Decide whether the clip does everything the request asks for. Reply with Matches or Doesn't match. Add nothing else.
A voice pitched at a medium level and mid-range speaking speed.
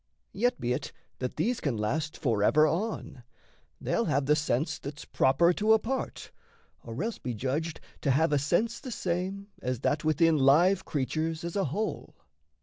Matches